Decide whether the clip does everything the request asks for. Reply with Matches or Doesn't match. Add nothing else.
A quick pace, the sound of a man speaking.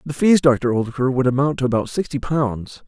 Matches